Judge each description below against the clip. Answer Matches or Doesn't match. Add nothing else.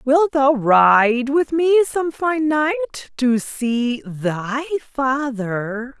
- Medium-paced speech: Doesn't match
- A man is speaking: Doesn't match